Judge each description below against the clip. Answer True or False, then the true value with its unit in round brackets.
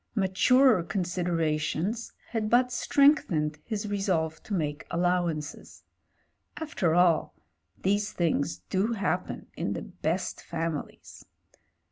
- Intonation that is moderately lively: True (4.7 semitones)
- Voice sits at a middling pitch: True (180 Hz)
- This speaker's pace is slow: True (110 wpm)